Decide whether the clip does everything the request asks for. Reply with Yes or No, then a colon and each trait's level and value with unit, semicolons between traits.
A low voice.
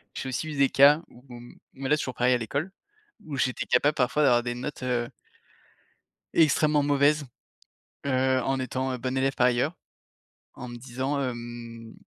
Yes: low, 130 Hz